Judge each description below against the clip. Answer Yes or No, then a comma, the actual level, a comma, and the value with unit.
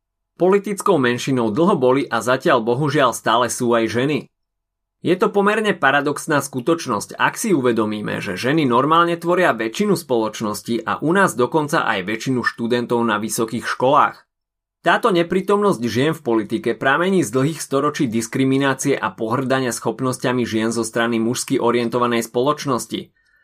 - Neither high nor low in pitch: No, low, 125 Hz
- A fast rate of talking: No, average, 140 wpm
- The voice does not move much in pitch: No, average, 4.5 semitones